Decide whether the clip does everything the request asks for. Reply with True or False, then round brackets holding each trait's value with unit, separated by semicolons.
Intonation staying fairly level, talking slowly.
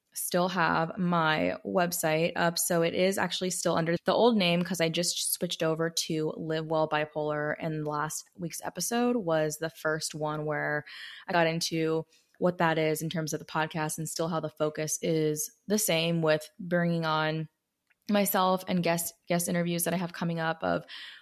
False (2.0 semitones; 185 wpm)